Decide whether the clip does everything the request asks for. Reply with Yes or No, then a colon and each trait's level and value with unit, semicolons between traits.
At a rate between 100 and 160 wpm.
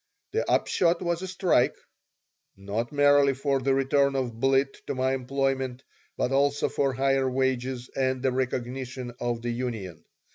Yes: average, 150 wpm